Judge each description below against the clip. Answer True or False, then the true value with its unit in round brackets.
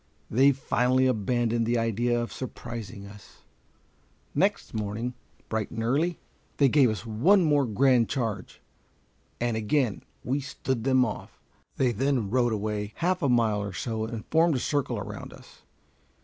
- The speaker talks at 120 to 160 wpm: True (150 wpm)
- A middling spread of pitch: True (3.3 semitones)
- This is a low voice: True (120 Hz)